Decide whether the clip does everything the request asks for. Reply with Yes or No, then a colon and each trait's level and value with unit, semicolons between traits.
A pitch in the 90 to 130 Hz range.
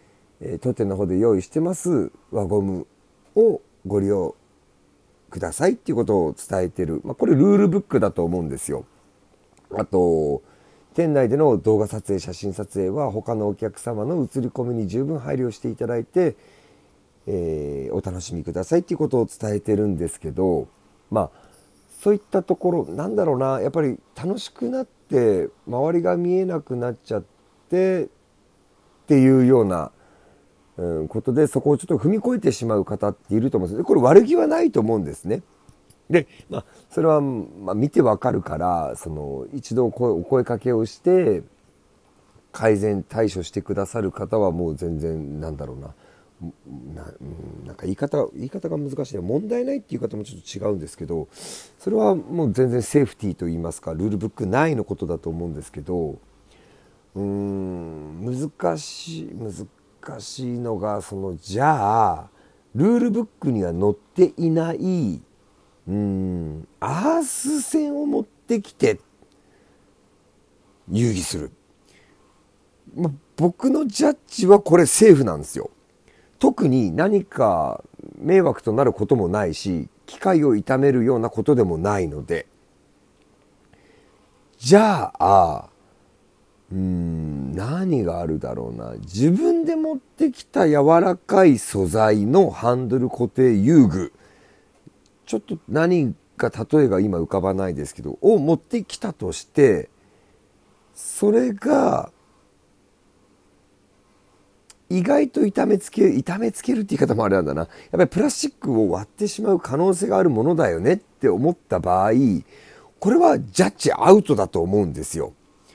Yes: low, 110 Hz